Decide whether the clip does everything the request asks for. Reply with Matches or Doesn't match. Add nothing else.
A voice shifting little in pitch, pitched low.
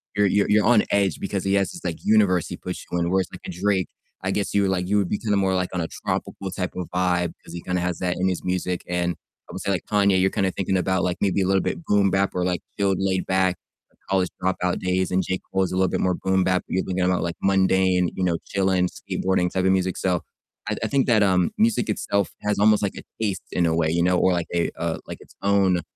Matches